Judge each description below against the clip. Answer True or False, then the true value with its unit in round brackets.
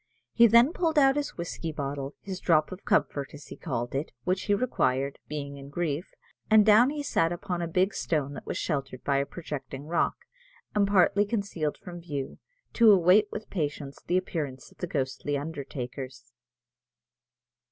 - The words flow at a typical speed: True (175 wpm)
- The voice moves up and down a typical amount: False (6.1 semitones)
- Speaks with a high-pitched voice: False (165 Hz)